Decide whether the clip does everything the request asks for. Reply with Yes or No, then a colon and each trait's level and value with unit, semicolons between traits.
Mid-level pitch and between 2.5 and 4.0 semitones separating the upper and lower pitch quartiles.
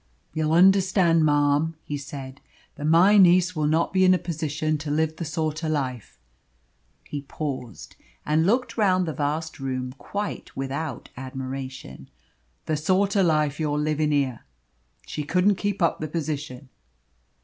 Yes: medium, 155 Hz; average, 3.3 semitones